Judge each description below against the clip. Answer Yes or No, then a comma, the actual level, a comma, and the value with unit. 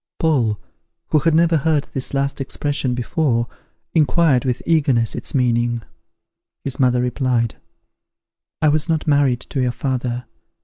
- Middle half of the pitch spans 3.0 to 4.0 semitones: Yes, average, 3.6 semitones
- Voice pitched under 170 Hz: Yes, low, 135 Hz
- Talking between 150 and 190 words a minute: No, slow, 135 wpm